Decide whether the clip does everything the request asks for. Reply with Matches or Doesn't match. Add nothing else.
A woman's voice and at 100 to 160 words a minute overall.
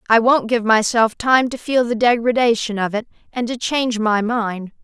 Doesn't match